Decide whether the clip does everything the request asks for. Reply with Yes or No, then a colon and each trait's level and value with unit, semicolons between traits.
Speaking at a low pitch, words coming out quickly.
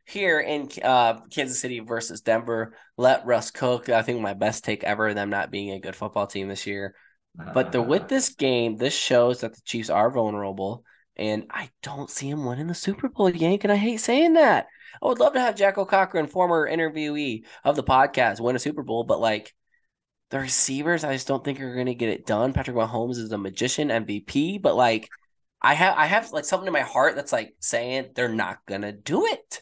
Yes: low, 130 Hz; fast, 220 wpm